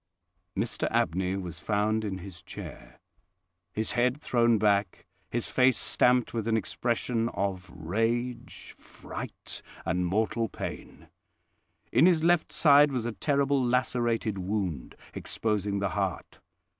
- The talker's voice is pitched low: Yes, low, 110 Hz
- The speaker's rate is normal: No, slow, 125 wpm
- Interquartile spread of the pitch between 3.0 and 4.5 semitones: Yes, average, 4.2 semitones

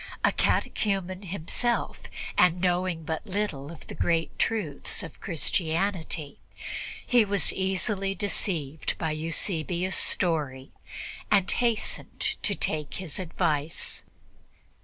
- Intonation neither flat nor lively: Yes, average, 3.6 semitones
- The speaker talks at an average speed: No, slow, 105 wpm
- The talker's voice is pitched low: No, medium, 175 Hz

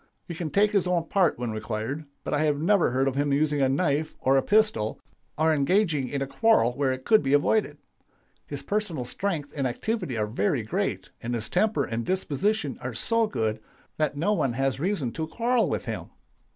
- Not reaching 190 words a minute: No, fast, 205 wpm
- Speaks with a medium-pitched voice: Yes, medium, 145 Hz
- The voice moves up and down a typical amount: No, wide, 6.5 semitones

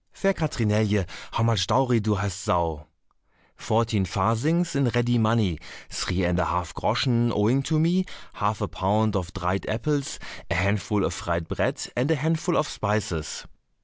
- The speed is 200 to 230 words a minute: No, average, 160 wpm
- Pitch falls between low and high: No, low, 110 Hz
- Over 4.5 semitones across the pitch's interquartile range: Yes, average, 5.2 semitones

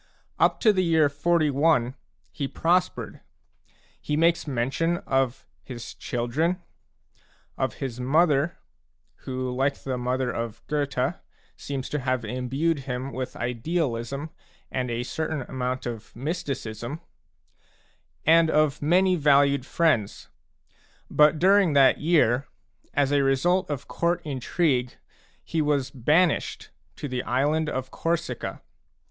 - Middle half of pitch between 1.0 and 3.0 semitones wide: No, average, 4.0 semitones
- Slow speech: Yes, slow, 120 wpm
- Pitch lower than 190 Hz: Yes, medium, 140 Hz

